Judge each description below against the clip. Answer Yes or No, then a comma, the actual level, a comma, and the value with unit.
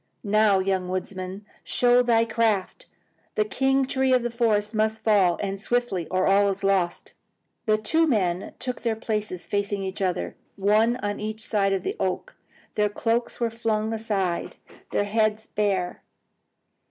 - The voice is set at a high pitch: Yes, high, 210 Hz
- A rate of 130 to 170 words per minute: Yes, average, 155 wpm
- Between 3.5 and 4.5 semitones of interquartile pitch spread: No, average, 2.8 semitones